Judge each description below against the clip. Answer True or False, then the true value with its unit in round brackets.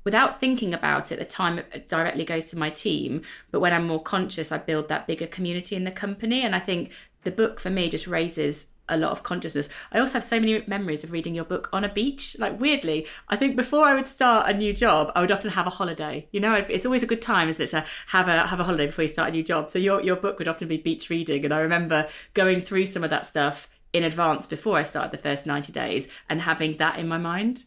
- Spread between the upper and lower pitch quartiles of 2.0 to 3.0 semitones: False (4.6 semitones)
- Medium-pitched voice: True (175 Hz)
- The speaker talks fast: True (260 wpm)